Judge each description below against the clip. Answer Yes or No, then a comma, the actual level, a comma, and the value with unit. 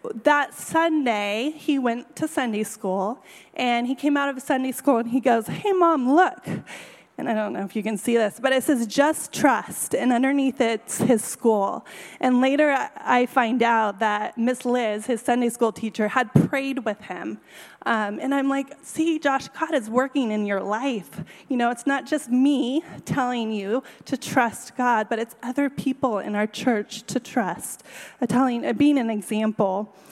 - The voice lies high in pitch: Yes, high, 245 Hz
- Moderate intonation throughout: Yes, average, 3.9 semitones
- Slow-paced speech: No, average, 185 wpm